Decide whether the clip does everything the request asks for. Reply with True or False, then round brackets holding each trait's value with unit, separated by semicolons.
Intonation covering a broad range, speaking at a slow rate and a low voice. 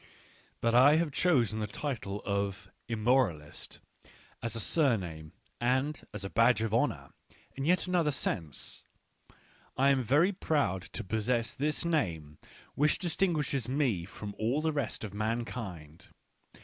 False (6.2 semitones; 145 wpm; 120 Hz)